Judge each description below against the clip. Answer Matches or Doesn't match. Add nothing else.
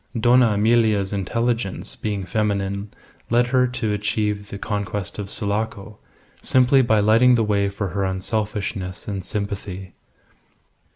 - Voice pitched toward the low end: Matches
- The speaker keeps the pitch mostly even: Matches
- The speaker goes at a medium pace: Doesn't match